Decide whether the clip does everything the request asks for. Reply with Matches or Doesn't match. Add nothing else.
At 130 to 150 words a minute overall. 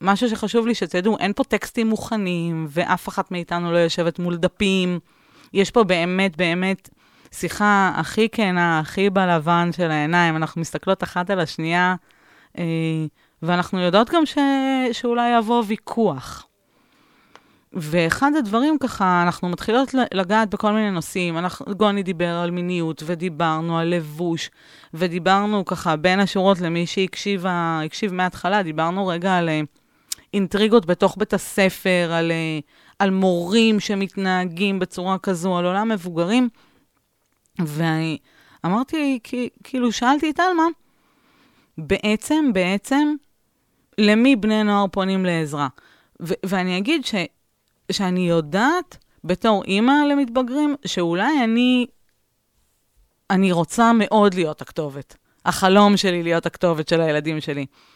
Doesn't match